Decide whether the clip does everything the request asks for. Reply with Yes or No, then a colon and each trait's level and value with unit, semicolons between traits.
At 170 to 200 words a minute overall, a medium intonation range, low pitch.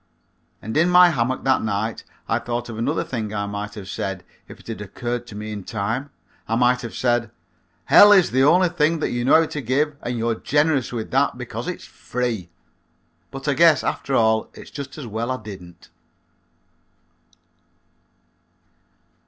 Yes: average, 175 wpm; average, 4.6 semitones; low, 120 Hz